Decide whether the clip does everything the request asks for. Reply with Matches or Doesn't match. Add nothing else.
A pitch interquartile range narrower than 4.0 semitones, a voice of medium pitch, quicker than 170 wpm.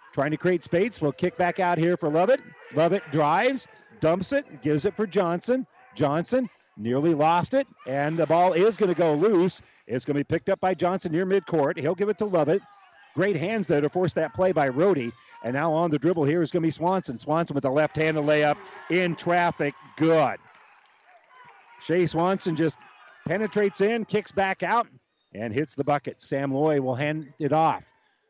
Doesn't match